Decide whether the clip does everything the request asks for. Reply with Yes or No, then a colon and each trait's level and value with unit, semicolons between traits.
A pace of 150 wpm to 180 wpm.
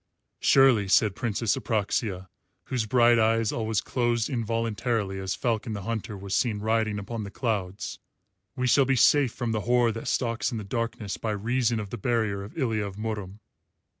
Yes: average, 175 wpm